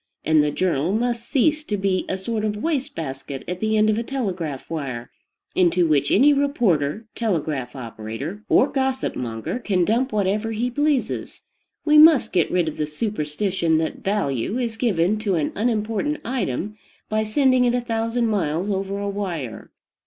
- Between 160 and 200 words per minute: Yes, average, 170 wpm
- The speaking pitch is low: No, high, 205 Hz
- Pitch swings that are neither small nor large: No, wide, 6.7 semitones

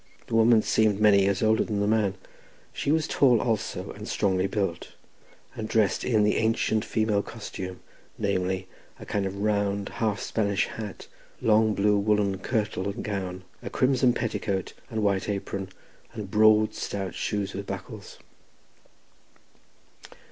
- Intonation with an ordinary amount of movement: No, narrow, 1.9 semitones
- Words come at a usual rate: Yes, average, 150 wpm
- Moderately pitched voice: No, low, 105 Hz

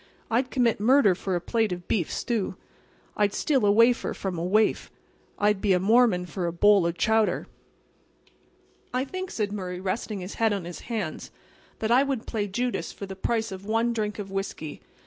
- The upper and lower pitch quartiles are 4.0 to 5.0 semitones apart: No, average, 3.6 semitones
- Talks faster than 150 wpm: Yes, average, 190 wpm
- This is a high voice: Yes, high, 210 Hz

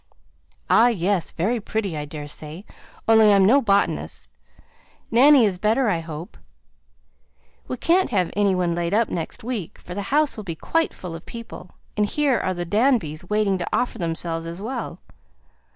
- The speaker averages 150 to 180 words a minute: Yes, average, 170 wpm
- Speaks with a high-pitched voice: Yes, high, 200 Hz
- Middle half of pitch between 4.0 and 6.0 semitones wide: Yes, average, 5.3 semitones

